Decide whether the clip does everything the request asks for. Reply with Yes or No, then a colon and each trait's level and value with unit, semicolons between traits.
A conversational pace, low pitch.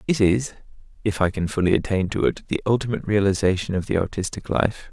Yes: average, 195 wpm; low, 100 Hz